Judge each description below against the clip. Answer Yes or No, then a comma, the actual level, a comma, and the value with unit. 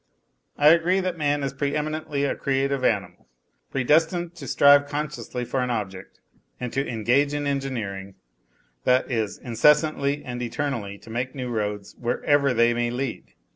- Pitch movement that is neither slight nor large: Yes, average, 3.6 semitones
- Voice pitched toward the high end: No, low, 135 Hz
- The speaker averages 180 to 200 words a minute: No, average, 155 wpm